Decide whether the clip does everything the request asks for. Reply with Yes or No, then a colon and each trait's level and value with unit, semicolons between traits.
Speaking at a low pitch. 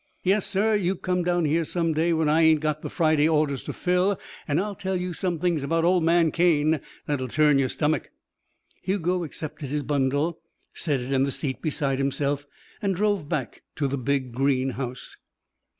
No: medium, 155 Hz